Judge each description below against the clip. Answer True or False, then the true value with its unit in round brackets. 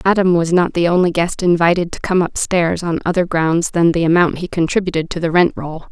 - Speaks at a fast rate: True (225 wpm)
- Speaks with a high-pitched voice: False (170 Hz)